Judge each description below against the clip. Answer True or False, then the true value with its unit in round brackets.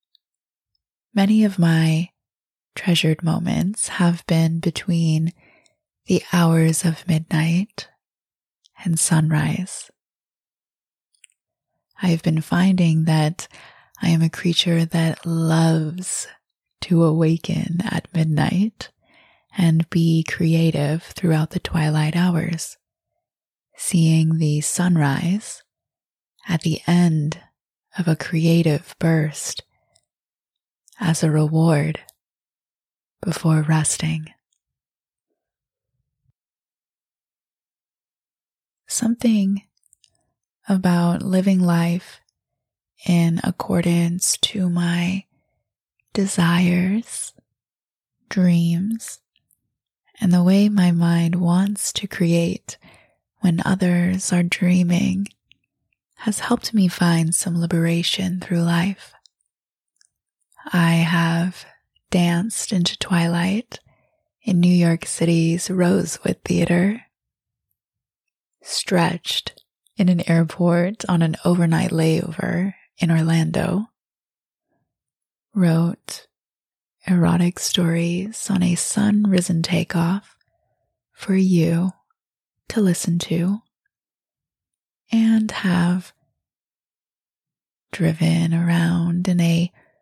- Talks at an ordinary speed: False (80 wpm)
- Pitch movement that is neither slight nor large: False (2.2 semitones)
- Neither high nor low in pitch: True (175 Hz)